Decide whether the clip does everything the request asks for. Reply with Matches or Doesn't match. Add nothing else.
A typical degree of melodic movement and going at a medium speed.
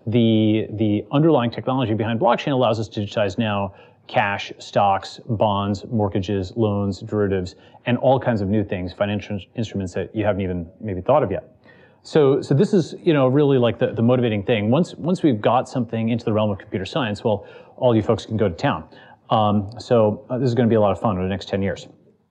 Doesn't match